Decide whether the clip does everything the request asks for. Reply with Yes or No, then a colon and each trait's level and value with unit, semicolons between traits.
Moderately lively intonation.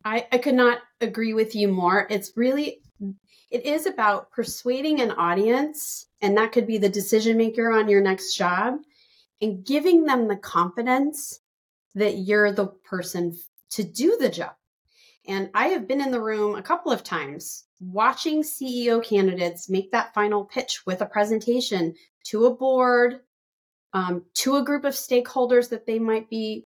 Yes: average, 4.1 semitones